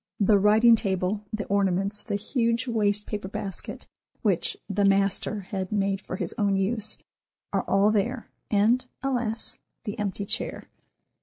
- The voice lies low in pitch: No, high, 205 Hz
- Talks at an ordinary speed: Yes, average, 145 wpm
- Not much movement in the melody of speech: Yes, narrow, 2.1 semitones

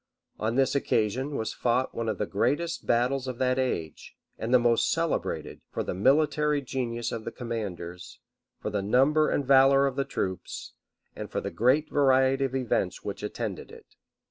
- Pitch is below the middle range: Yes, low, 130 Hz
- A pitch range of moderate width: Yes, average, 3.3 semitones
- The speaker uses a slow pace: No, average, 175 wpm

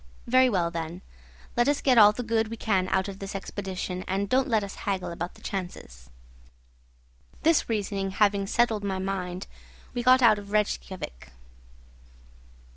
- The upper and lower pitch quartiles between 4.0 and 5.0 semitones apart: No, average, 3.4 semitones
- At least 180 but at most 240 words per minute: No, average, 160 wpm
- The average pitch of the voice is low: No, high, 200 Hz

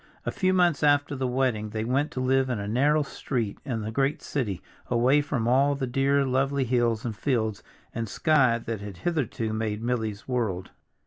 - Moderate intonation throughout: Yes, average, 3.9 semitones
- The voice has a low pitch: Yes, low, 125 Hz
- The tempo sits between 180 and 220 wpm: Yes, average, 190 wpm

